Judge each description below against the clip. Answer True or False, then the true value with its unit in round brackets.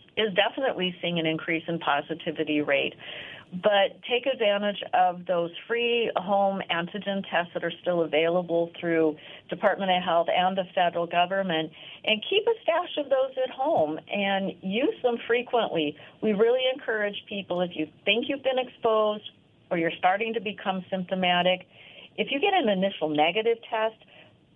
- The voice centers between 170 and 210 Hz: True (190 Hz)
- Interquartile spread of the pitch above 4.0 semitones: True (5.0 semitones)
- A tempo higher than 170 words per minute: False (155 wpm)